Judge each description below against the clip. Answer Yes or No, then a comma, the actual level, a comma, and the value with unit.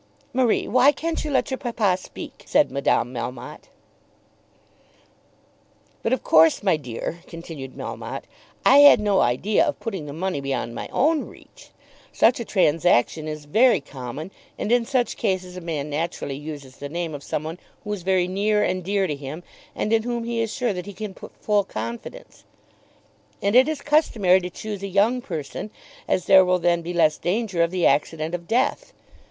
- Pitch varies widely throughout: Yes, wide, 6.3 semitones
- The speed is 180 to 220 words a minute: Yes, average, 185 wpm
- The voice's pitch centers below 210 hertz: Yes, medium, 185 Hz